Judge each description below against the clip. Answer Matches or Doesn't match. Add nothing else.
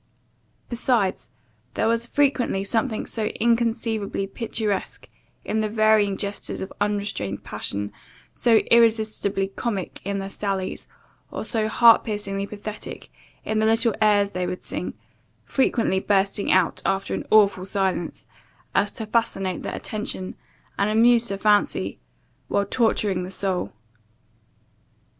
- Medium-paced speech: Doesn't match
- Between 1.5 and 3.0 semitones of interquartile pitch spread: Matches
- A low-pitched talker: Doesn't match